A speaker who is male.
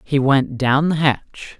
Yes: male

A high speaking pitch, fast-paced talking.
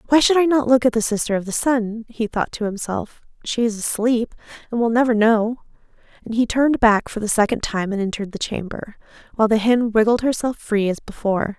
Yes: high, 225 Hz; fast, 220 wpm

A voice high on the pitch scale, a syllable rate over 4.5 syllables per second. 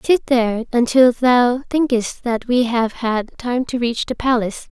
No: high, 240 Hz; 4.2 syllables/s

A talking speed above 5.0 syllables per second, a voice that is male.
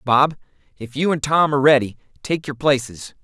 Yes: 5.3 syllables/s; male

